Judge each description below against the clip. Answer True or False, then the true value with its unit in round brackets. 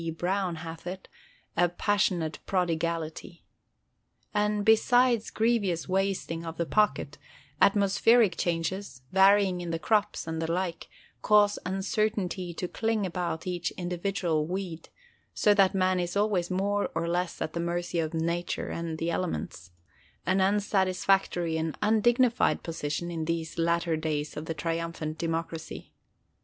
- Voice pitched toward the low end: False (175 Hz)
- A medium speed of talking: False (130 wpm)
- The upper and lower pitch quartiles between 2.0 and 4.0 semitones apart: True (3.2 semitones)